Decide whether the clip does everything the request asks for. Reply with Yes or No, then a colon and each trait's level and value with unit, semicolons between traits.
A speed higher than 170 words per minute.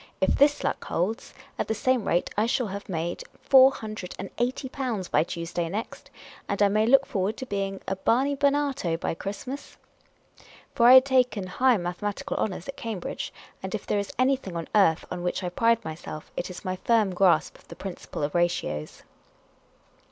Yes: average, 190 wpm